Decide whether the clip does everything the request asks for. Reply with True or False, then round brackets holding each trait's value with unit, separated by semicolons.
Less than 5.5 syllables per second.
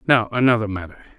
False (6.5 syllables/s)